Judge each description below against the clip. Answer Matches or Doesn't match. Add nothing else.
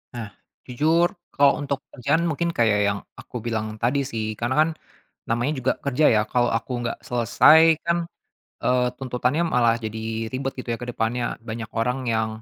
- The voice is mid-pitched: Doesn't match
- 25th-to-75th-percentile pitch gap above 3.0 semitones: Matches